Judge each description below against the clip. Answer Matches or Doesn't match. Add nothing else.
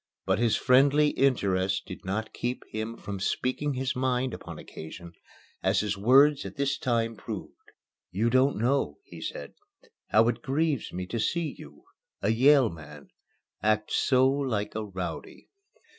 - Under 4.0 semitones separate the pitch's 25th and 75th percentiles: Doesn't match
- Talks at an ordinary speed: Matches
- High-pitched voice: Doesn't match